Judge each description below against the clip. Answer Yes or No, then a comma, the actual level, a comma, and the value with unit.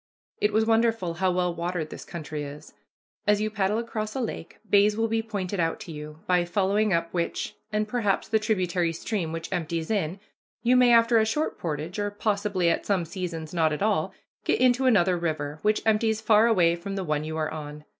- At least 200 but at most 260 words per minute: Yes, fast, 205 wpm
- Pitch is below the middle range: No, high, 190 Hz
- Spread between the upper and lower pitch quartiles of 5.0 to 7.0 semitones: No, average, 4.5 semitones